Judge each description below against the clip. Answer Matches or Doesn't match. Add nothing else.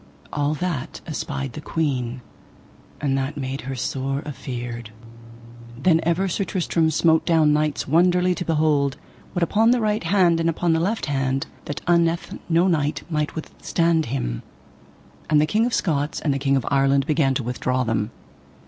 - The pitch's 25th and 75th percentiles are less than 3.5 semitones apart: Doesn't match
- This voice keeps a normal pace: Matches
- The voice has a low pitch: Doesn't match